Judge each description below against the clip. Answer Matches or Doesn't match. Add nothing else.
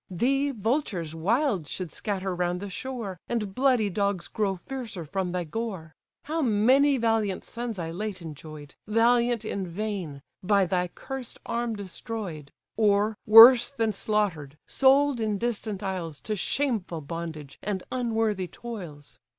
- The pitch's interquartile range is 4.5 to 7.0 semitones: Matches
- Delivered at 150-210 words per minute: Doesn't match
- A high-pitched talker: Matches